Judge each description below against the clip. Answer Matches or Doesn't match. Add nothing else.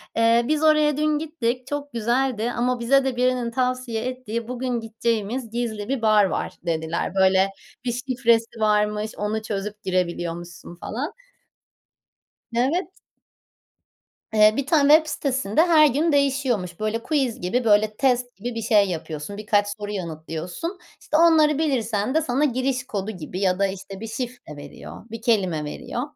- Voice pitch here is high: Matches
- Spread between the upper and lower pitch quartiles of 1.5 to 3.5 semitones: Doesn't match